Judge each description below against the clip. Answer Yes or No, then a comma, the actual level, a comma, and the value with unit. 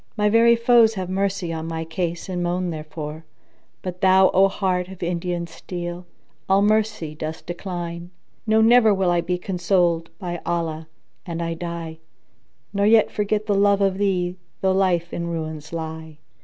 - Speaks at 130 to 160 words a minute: No, average, 170 wpm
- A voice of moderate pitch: Yes, medium, 180 Hz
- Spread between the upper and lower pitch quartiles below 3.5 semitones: Yes, average, 2.7 semitones